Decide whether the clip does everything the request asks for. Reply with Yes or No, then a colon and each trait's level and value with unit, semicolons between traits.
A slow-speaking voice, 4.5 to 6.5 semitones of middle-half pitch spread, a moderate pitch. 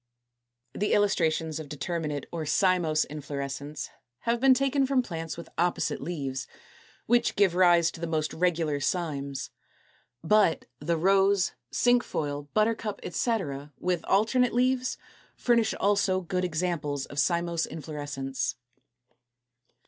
Yes: slow, 120 wpm; average, 5.3 semitones; medium, 170 Hz